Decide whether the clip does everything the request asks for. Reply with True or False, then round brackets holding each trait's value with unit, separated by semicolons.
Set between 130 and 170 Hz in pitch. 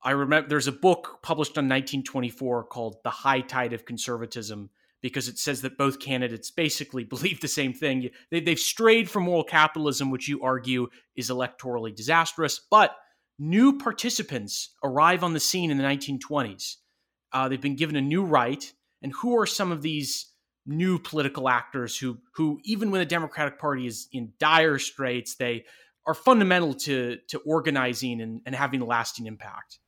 True (140 Hz)